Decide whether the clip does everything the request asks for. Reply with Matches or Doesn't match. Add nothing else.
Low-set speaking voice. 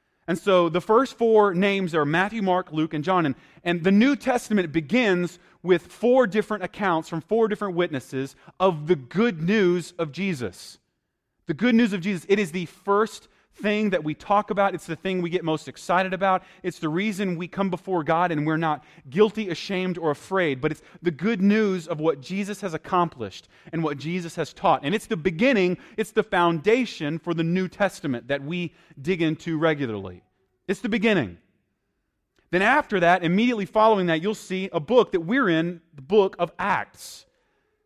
Doesn't match